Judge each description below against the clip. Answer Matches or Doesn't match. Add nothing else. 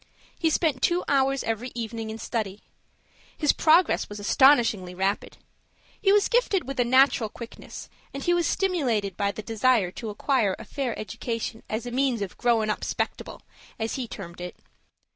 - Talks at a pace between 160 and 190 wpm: Matches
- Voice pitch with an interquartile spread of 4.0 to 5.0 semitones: Matches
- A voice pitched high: Matches